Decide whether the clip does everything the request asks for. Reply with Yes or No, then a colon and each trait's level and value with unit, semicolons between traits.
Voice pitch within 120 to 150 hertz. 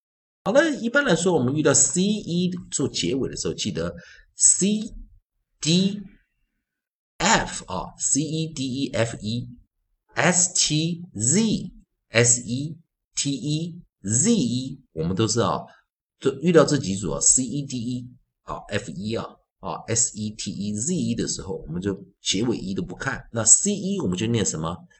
Yes: medium, 140 Hz